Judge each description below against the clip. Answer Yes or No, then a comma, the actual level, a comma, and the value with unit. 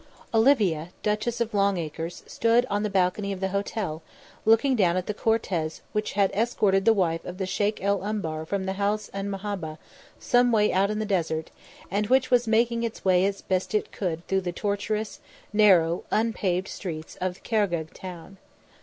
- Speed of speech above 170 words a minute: Yes, average, 180 wpm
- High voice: Yes, high, 200 Hz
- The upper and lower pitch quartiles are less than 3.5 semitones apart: Yes, average, 3.0 semitones